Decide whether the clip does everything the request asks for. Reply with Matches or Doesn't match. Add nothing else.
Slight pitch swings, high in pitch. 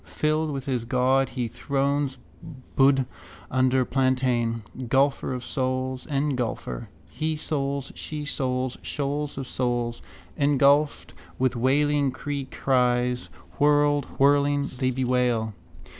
Doesn't match